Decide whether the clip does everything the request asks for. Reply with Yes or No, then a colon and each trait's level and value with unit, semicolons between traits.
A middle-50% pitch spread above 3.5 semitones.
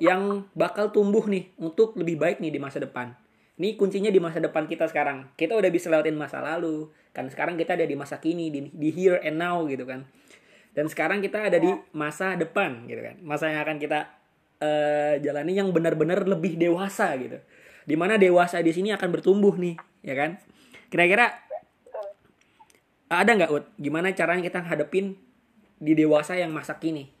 Yes: average, 4.0 semitones